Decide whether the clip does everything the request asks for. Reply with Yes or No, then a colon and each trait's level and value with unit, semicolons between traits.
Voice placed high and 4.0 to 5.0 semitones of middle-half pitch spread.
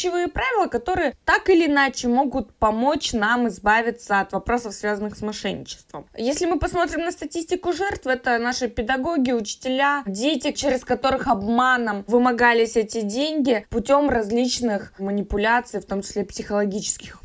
Yes: high, 245 Hz; average, 4.7 semitones